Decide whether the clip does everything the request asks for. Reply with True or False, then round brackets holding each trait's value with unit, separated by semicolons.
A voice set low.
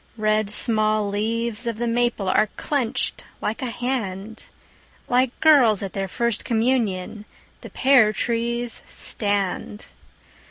False (225 Hz)